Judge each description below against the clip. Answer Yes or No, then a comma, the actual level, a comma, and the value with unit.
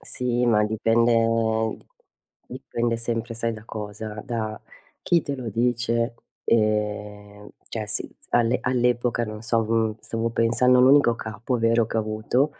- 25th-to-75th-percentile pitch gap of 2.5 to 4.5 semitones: No, narrow, 1.6 semitones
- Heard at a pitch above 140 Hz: No, low, 115 Hz